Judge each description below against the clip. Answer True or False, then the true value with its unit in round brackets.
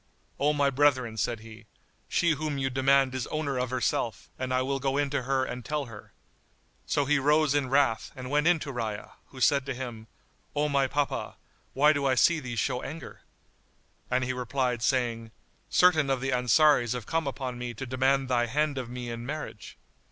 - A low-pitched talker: True (130 Hz)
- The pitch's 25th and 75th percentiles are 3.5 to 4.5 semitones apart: False (2.6 semitones)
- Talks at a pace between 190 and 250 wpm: True (200 wpm)